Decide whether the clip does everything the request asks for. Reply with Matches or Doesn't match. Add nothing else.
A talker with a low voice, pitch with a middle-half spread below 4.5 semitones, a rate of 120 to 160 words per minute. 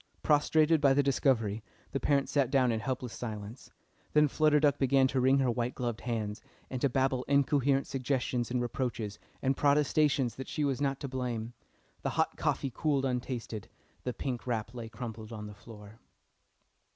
Doesn't match